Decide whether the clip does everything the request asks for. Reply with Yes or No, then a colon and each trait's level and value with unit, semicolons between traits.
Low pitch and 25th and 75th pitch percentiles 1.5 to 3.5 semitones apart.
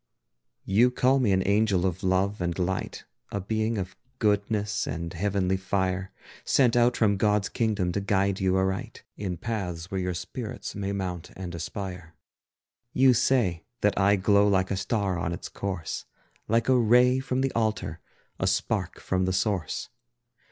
Yes: low, 100 Hz; average, 2.8 semitones